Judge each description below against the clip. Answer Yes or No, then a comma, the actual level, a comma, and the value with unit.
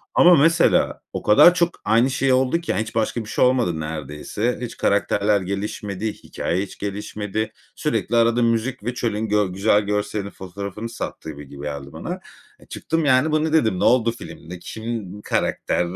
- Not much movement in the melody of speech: No, average, 3.7 semitones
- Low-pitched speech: Yes, low, 105 Hz